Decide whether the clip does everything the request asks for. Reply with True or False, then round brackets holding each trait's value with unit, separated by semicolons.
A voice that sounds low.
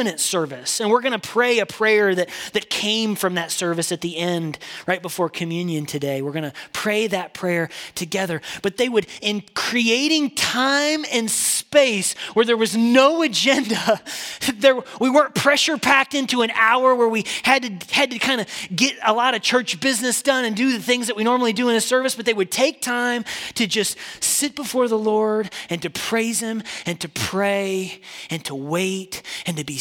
False (220 Hz)